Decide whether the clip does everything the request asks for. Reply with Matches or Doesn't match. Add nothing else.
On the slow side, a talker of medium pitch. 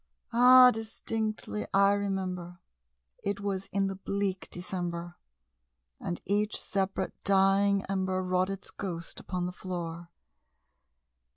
Doesn't match